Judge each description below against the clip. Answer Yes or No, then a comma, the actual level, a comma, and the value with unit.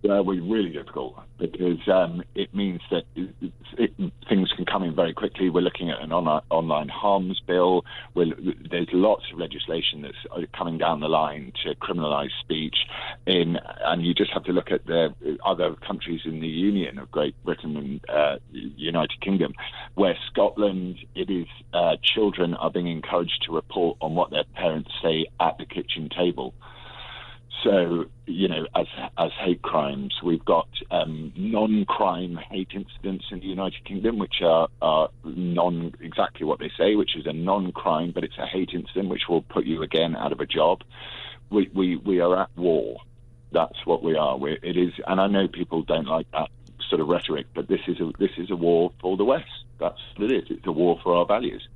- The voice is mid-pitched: No, very low, 90 Hz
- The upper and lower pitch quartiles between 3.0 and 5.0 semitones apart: No, narrow, 2.6 semitones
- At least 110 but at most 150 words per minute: No, average, 190 wpm